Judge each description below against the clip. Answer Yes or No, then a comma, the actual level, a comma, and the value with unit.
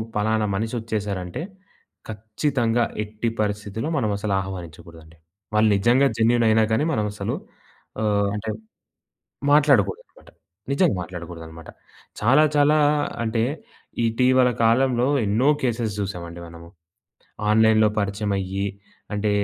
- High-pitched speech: No, low, 110 Hz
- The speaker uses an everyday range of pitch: Yes, average, 3.1 semitones